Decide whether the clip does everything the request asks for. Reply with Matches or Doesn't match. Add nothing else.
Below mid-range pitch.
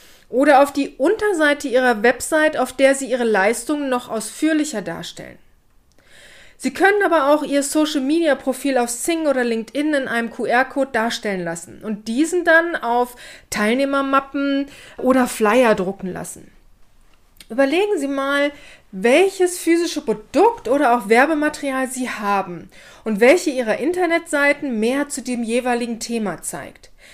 Doesn't match